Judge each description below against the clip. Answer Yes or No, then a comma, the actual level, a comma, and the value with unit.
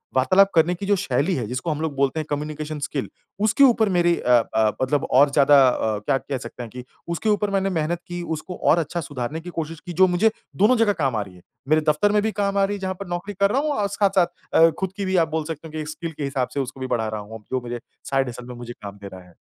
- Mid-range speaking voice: Yes, medium, 160 Hz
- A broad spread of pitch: Yes, wide, 6.6 semitones